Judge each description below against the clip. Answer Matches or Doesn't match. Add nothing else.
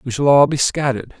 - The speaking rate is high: Matches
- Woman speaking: Doesn't match